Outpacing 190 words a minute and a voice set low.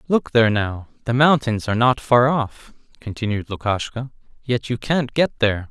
No: average, 170 wpm; low, 120 Hz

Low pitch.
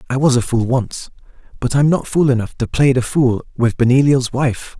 Yes: low, 130 Hz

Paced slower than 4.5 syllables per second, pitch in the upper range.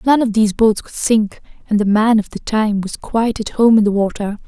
No: 5.5 syllables/s; high, 215 Hz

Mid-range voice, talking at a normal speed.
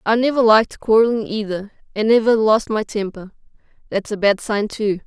No: high, 215 Hz; average, 165 wpm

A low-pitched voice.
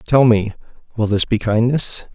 Yes: low, 115 Hz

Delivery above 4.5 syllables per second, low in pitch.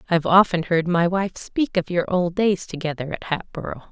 No: 5.2 syllables/s; medium, 175 Hz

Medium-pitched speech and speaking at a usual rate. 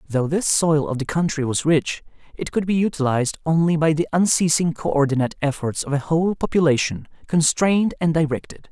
Yes: medium, 155 Hz; average, 180 wpm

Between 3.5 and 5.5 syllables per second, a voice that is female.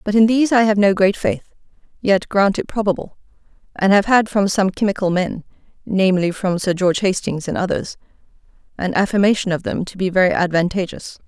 No: 5.8 syllables/s; female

